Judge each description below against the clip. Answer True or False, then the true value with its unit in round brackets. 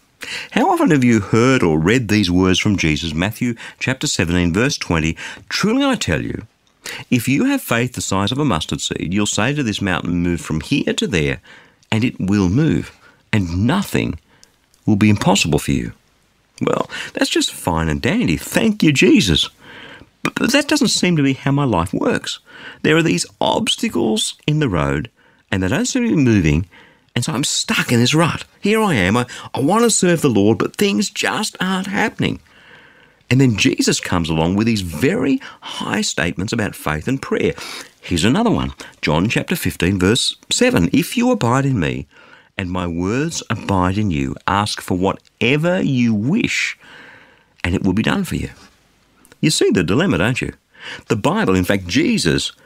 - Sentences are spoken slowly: False (185 wpm)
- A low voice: True (115 Hz)